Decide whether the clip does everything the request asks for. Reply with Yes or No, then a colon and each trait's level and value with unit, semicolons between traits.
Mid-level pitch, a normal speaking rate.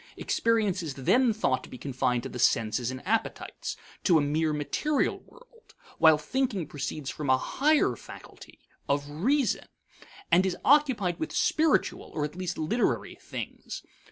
Yes: medium, 170 Hz; average, 155 wpm